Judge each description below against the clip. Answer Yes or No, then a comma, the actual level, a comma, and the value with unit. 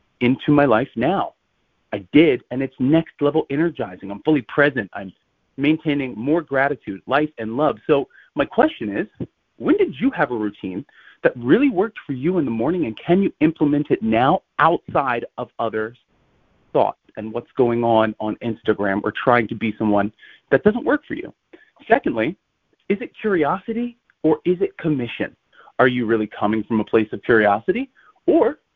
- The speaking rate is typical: Yes, average, 175 wpm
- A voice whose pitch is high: No, medium, 140 Hz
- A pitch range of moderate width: No, wide, 7.5 semitones